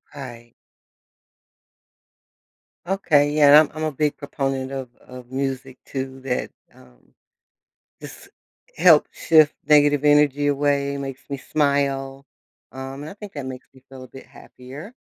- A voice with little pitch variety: Yes, narrow, 1.8 semitones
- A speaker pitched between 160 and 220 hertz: No, medium, 140 Hz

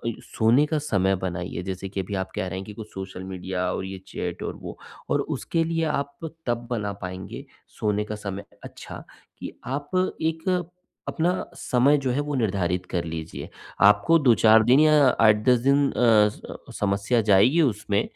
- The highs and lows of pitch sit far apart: Yes, wide, 6.5 semitones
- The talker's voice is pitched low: Yes, low, 110 Hz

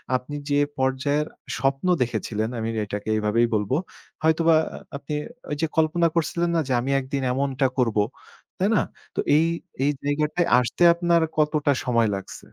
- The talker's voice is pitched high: No, medium, 140 Hz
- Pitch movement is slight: No, average, 4.4 semitones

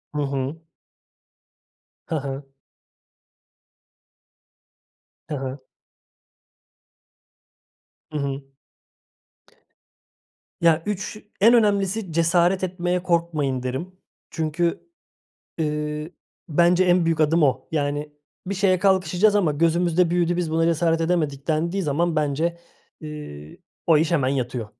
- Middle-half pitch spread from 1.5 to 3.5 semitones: Yes, average, 3.1 semitones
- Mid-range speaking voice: Yes, medium, 165 Hz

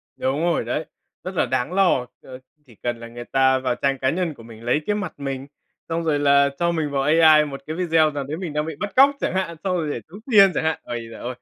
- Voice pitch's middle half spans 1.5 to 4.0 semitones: No, average, 4.4 semitones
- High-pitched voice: No, medium, 150 Hz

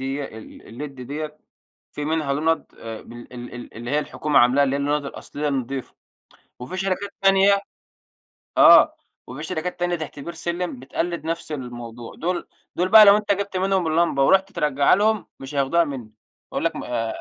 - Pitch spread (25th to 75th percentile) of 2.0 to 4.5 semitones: No, average, 5.0 semitones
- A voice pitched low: No, medium, 150 Hz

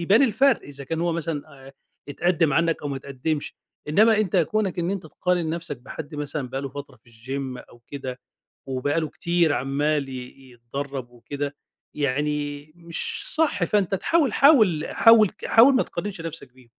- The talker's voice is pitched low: No, medium, 150 Hz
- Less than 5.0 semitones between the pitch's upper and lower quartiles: Yes, average, 4.5 semitones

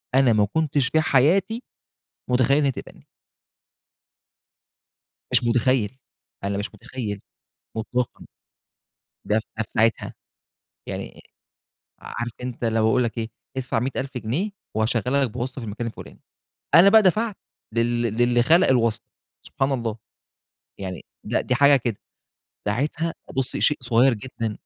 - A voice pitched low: Yes, low, 125 Hz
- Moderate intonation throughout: Yes, average, 3.2 semitones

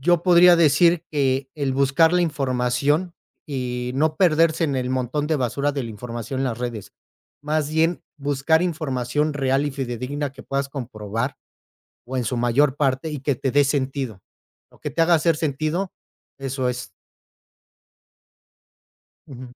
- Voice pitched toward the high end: No, medium, 140 Hz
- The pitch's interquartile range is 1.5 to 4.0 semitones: Yes, average, 3.4 semitones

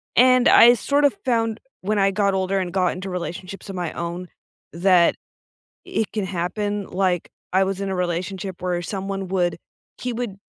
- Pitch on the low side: No, high, 190 Hz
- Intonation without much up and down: Yes, narrow, 2.3 semitones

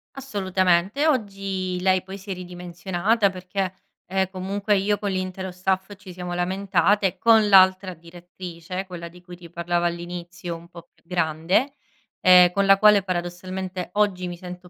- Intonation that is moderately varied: No, narrow, 1.8 semitones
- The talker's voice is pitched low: No, medium, 185 Hz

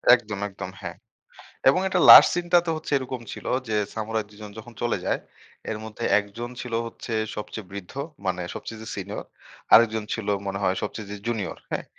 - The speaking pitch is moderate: No, low, 110 Hz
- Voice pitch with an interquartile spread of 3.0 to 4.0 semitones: No, narrow, 2.6 semitones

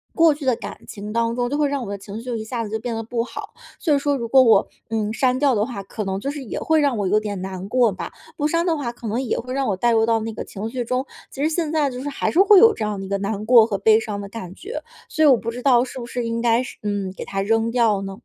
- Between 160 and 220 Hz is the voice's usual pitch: No, high, 230 Hz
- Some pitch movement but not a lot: Yes, average, 4.1 semitones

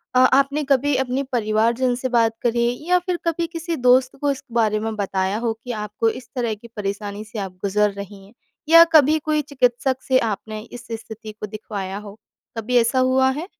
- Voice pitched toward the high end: Yes, high, 235 Hz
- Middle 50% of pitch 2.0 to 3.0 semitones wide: No, average, 3.8 semitones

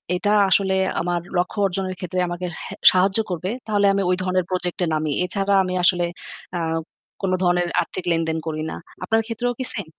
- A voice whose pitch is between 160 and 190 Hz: Yes, medium, 185 Hz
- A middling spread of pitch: No, narrow, 1.9 semitones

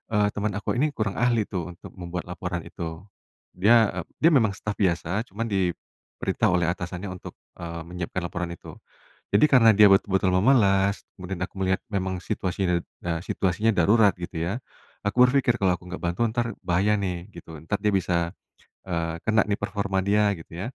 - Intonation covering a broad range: No, average, 3.2 semitones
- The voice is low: Yes, very low, 95 Hz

